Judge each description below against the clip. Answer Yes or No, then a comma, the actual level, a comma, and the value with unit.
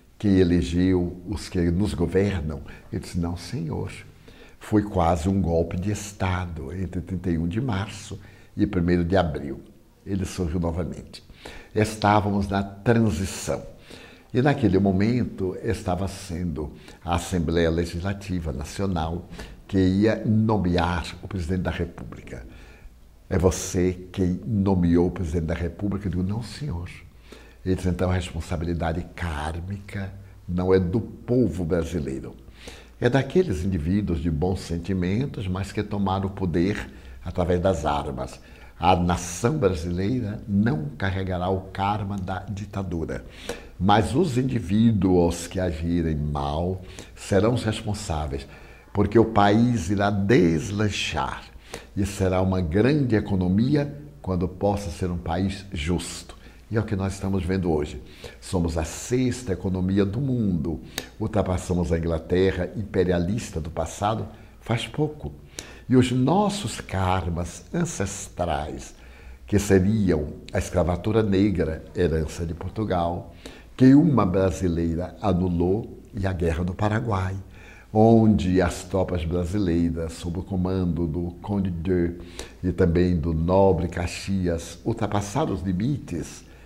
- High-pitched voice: No, very low, 95 Hz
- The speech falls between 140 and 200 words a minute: No, average, 125 wpm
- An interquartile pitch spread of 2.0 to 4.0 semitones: Yes, average, 3.0 semitones